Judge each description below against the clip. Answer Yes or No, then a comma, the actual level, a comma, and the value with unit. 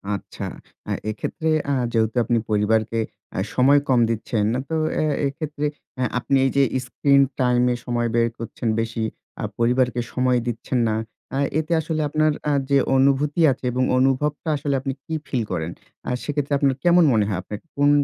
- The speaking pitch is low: Yes, low, 130 Hz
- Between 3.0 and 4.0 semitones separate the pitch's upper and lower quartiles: Yes, average, 3.6 semitones